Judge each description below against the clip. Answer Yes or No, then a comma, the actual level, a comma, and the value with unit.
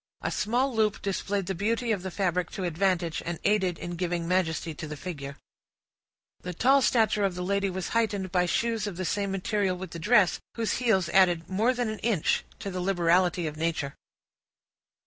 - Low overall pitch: No, high, 190 Hz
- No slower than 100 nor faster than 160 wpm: No, average, 190 wpm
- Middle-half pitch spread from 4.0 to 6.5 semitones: No, average, 3.3 semitones